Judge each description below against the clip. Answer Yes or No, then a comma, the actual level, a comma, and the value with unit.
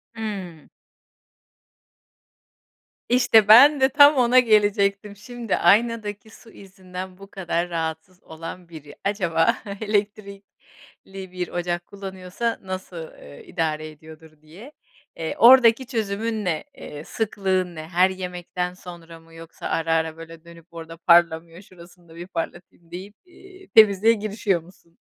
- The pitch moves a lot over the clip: No, average, 4.2 semitones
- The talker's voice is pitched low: No, medium, 185 Hz